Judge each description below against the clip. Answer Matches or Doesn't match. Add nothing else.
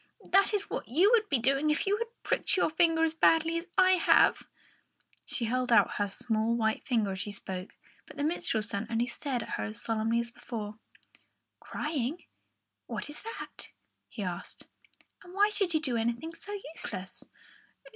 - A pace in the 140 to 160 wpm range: Doesn't match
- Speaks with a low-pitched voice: Doesn't match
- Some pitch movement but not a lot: Doesn't match